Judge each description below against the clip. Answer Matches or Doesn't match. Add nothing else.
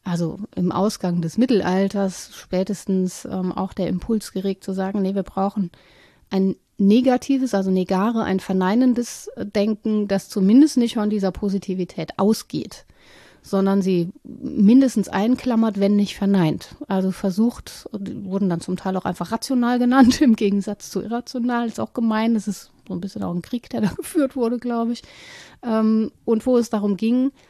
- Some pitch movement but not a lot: Matches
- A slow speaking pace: Doesn't match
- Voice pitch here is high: Matches